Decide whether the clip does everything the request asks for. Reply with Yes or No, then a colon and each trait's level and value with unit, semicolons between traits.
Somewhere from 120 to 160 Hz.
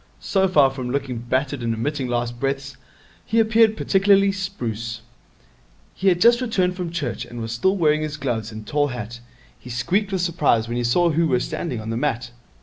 Yes: medium, 140 Hz